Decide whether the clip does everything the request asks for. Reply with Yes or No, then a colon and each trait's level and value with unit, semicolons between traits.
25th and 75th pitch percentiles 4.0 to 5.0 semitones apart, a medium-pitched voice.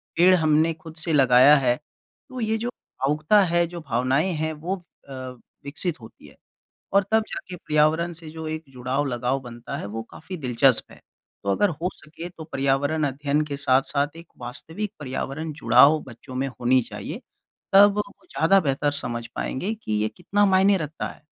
Yes: average, 4.6 semitones; medium, 150 Hz